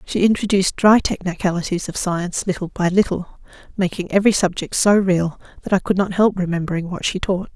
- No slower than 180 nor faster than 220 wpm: Yes, average, 185 wpm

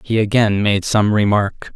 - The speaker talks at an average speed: Yes, average, 170 wpm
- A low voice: Yes, low, 105 Hz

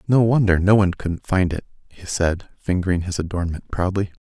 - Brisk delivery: No, average, 185 wpm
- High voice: No, very low, 90 Hz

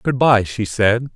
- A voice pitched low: Yes, low, 115 Hz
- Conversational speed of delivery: No, fast, 210 wpm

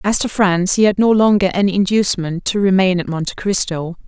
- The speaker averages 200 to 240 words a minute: Yes, fast, 205 wpm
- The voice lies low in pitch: No, high, 190 Hz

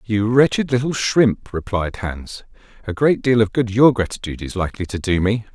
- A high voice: No, low, 110 Hz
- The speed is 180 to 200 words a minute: Yes, average, 195 wpm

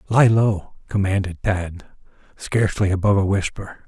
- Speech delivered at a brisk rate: No, slow, 125 wpm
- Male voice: Yes, male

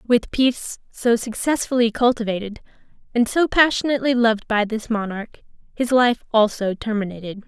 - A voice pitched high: Yes, high, 230 Hz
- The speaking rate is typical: No, slow, 130 wpm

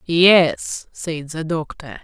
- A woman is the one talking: Yes, female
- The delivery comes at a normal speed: No, slow, 120 wpm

